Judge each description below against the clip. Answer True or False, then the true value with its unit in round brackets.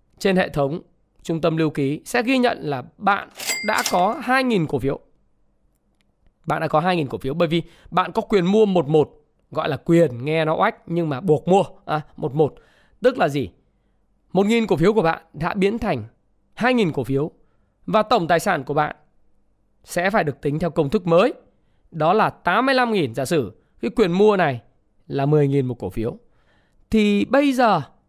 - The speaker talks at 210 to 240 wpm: False (195 wpm)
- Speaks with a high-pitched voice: False (170 Hz)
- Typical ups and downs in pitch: False (6.2 semitones)